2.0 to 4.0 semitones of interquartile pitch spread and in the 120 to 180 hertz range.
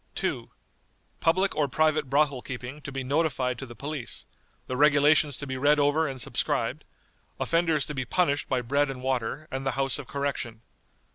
Yes: narrow, 2.5 semitones; medium, 140 Hz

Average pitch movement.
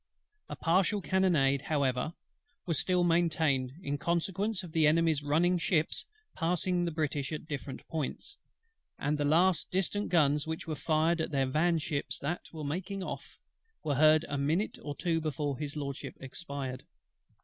Yes: average, 3.3 semitones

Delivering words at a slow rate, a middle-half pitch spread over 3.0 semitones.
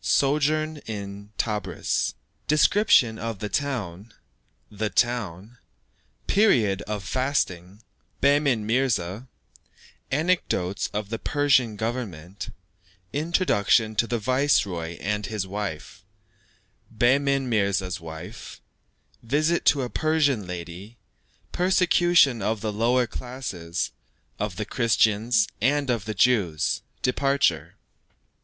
Yes: slow, 100 wpm; wide, 5.4 semitones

